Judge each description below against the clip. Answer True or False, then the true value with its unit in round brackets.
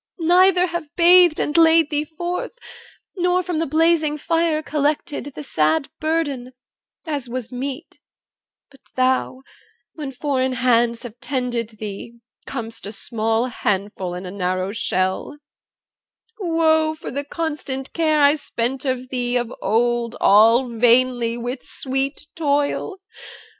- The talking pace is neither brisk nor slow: False (130 wpm)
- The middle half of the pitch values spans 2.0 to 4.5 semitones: False (5.0 semitones)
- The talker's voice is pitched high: True (265 Hz)